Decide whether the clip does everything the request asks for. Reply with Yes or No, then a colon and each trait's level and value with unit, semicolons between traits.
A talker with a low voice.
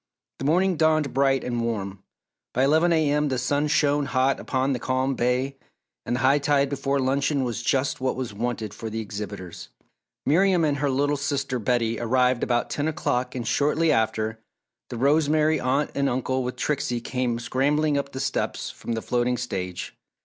Yes: low, 130 Hz